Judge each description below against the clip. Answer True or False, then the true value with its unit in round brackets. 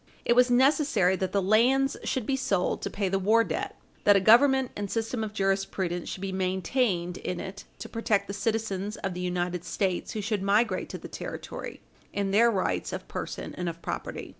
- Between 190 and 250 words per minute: True (200 wpm)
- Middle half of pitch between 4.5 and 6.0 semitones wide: False (3.5 semitones)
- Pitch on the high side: True (200 Hz)